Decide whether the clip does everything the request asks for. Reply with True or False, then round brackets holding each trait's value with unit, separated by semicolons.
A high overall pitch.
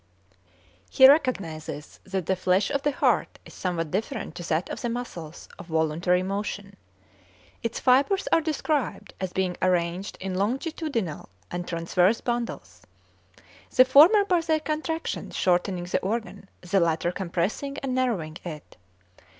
True (195 Hz)